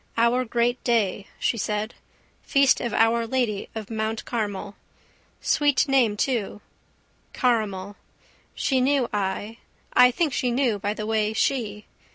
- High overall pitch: Yes, high, 230 Hz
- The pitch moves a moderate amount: Yes, average, 3.0 semitones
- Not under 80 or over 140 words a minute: Yes, slow, 135 wpm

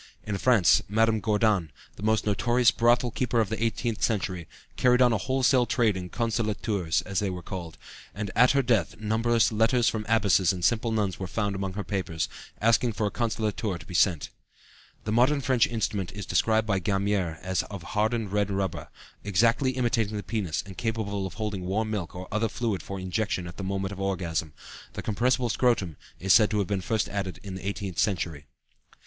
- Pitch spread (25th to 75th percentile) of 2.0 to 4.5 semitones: Yes, average, 3.1 semitones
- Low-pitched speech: Yes, low, 105 Hz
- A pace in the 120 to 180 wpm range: No, average, 195 wpm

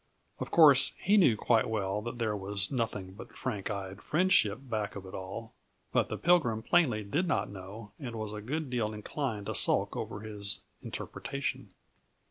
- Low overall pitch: Yes, low, 110 Hz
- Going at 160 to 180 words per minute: Yes, average, 175 wpm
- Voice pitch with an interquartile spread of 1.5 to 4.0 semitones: No, average, 4.7 semitones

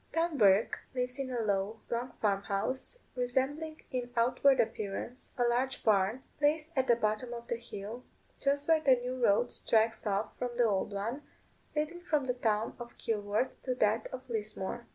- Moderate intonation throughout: Yes, average, 3.5 semitones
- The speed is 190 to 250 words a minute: No, average, 175 wpm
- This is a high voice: Yes, high, 240 Hz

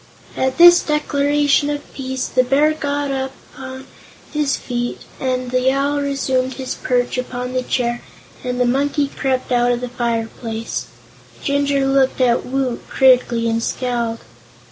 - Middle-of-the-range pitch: No, very high, 260 Hz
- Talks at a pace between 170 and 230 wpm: No, average, 145 wpm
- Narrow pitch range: Yes, narrow, 2.2 semitones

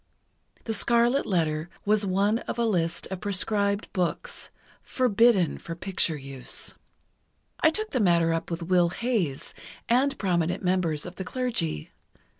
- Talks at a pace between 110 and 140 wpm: Yes, slow, 135 wpm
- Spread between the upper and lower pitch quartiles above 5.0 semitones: Yes, wide, 5.5 semitones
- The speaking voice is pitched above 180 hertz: Yes, high, 190 Hz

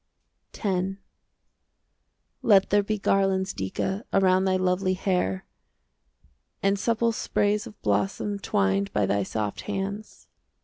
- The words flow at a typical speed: No, slow, 115 wpm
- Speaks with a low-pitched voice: No, high, 190 Hz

